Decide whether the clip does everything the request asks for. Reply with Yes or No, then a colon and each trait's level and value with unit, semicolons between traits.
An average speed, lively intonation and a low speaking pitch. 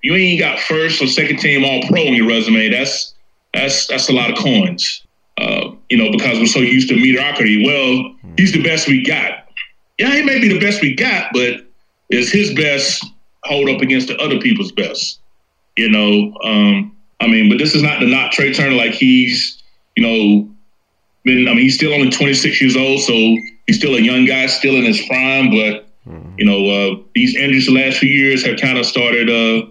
No: fast, 210 wpm; wide, 6.9 semitones; low, 130 Hz